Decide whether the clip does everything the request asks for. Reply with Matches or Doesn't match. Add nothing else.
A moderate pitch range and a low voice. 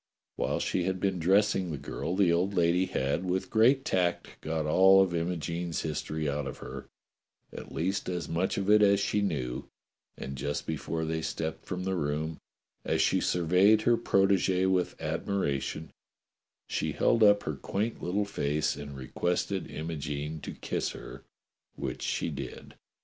Matches